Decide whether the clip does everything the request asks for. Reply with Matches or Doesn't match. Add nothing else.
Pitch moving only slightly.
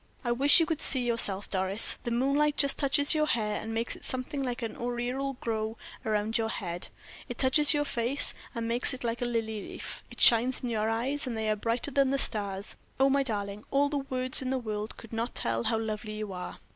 Doesn't match